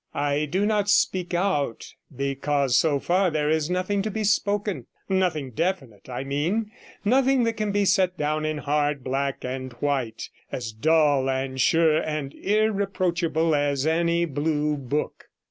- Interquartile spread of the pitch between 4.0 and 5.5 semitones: Yes, average, 5.1 semitones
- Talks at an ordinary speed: Yes, average, 150 wpm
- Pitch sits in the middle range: Yes, medium, 155 Hz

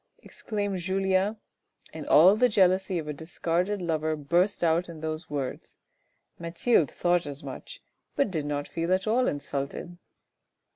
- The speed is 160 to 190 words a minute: No, average, 150 wpm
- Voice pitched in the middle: Yes, medium, 175 Hz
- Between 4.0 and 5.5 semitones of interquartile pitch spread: No, average, 3.5 semitones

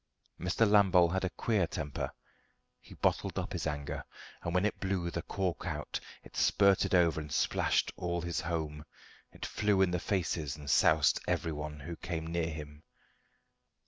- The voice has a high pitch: No, very low, 85 Hz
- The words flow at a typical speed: Yes, average, 165 wpm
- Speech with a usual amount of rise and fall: Yes, average, 3.4 semitones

